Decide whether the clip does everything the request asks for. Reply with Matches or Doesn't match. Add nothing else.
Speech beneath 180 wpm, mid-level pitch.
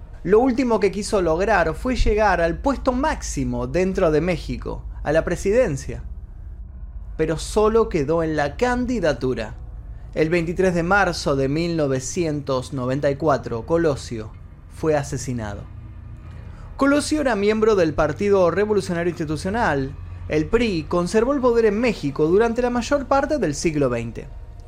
Matches